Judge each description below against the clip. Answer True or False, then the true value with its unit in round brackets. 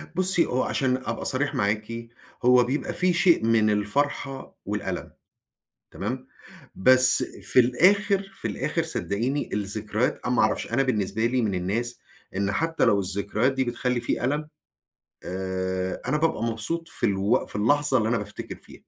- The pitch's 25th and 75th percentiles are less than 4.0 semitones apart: False (4.7 semitones)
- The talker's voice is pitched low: True (120 Hz)